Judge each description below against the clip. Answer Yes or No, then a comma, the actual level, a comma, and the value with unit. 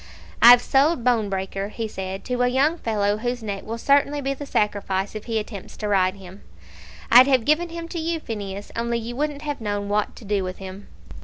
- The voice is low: No, high, 225 Hz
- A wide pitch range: No, average, 5.0 semitones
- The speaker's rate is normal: No, fast, 210 wpm